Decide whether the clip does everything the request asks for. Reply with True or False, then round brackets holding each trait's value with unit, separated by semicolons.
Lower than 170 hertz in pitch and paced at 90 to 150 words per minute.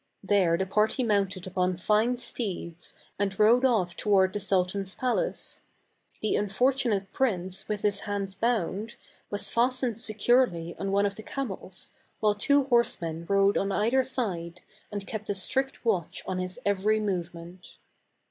False (200 Hz; 145 wpm)